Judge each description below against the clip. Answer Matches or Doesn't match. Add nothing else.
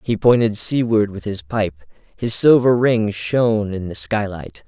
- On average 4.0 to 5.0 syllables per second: Matches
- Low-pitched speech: Matches